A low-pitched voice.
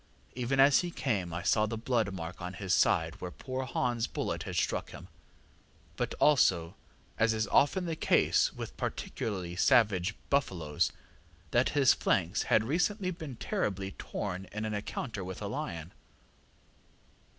Yes: low, 110 Hz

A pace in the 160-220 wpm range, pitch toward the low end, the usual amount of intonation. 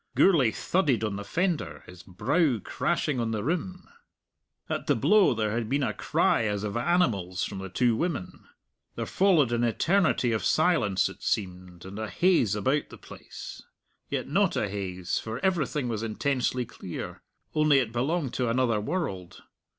No: average, 165 wpm; low, 120 Hz; wide, 6.9 semitones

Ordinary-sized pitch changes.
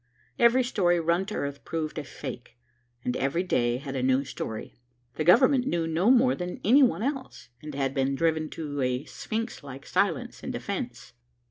No: wide, 7.7 semitones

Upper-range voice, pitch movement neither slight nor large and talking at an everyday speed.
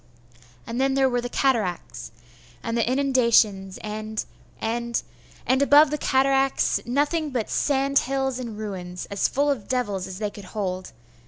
Yes: high, 240 Hz; average, 4.5 semitones; average, 155 wpm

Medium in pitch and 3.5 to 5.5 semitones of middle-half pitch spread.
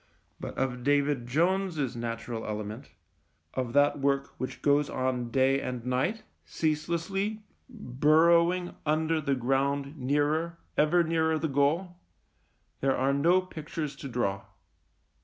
Yes: medium, 145 Hz; average, 4.1 semitones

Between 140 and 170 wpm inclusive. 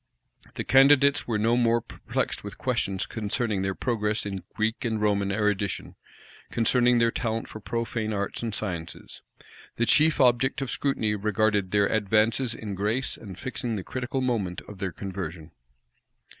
Yes: average, 155 wpm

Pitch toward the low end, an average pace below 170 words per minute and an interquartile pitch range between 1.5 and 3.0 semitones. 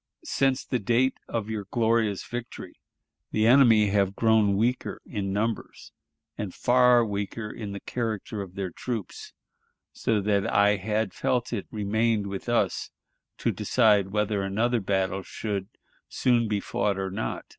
Yes: low, 105 Hz; average, 145 wpm; average, 2.7 semitones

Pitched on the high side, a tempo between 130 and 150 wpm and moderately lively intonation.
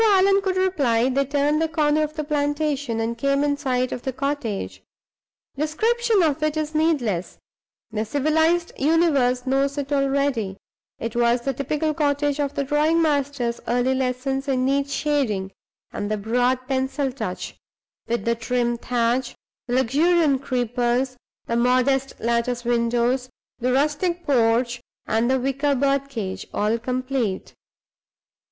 Yes: very high, 270 Hz; average, 145 wpm; average, 3.5 semitones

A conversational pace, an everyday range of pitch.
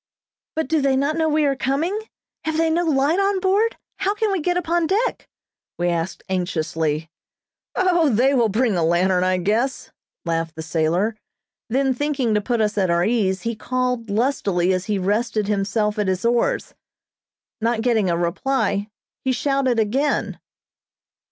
No: average, 165 wpm; wide, 7.6 semitones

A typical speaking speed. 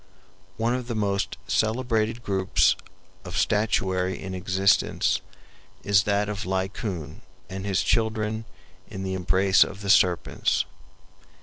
No: slow, 120 wpm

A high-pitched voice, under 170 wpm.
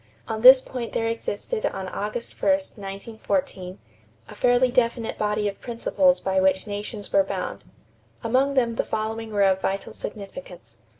Yes: high, 220 Hz; average, 155 wpm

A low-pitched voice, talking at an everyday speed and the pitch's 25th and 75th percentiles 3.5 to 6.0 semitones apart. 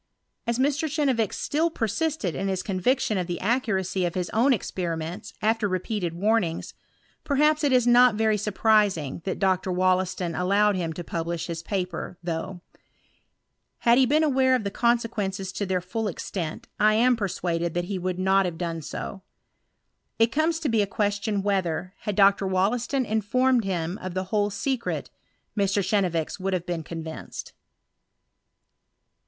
No: high, 200 Hz; average, 160 wpm; average, 4.1 semitones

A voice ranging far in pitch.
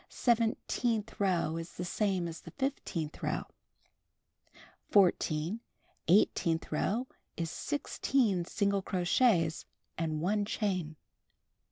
No: average, 4.6 semitones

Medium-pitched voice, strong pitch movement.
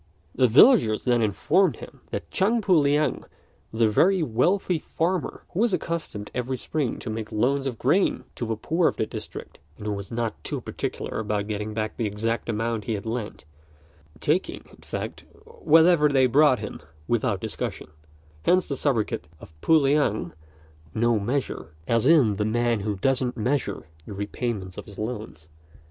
No: low, 120 Hz; wide, 5.8 semitones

